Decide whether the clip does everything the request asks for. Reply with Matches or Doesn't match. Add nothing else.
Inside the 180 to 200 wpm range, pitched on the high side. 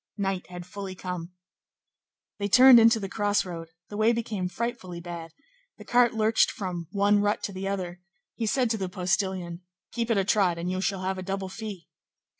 Matches